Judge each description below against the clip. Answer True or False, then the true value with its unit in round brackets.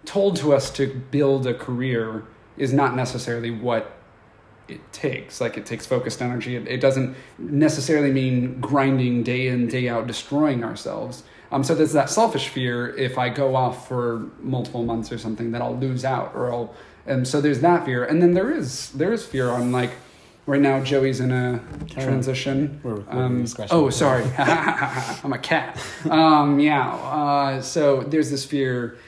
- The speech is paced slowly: False (175 wpm)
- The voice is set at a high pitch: False (130 Hz)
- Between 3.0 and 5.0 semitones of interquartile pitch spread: False (2.4 semitones)